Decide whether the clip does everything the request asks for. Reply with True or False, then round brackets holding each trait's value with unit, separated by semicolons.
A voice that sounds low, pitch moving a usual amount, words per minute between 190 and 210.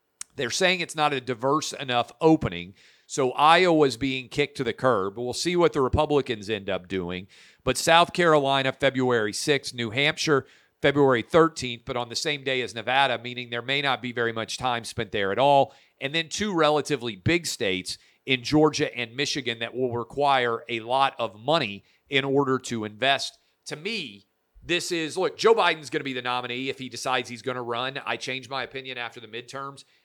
True (130 Hz; 3.6 semitones; 195 wpm)